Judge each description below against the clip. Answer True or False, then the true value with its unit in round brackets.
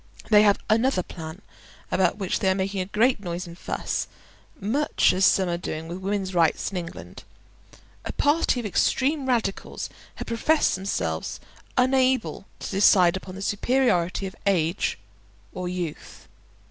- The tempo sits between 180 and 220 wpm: False (150 wpm)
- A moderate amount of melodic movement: True (4.2 semitones)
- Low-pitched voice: False (195 Hz)